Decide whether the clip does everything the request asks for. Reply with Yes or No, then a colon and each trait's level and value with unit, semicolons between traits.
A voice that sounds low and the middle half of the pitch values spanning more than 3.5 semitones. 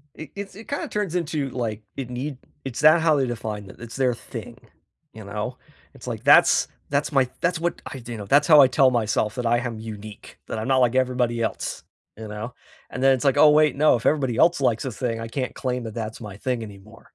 Yes: low, 125 Hz; average, 4.0 semitones